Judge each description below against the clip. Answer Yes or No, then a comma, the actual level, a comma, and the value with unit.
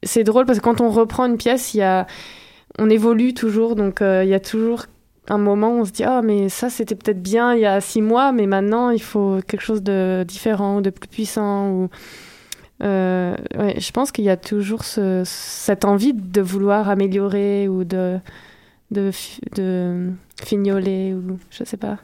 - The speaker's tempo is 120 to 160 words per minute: No, average, 210 wpm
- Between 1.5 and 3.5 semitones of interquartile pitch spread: Yes, average, 2.8 semitones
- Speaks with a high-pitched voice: Yes, high, 205 Hz